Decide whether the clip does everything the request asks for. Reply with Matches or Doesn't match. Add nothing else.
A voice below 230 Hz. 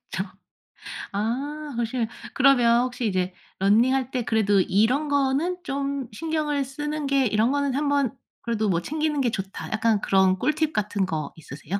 Doesn't match